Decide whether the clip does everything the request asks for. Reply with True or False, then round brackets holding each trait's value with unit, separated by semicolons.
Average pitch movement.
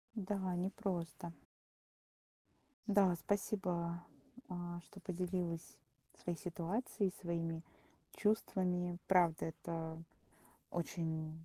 False (2.1 semitones)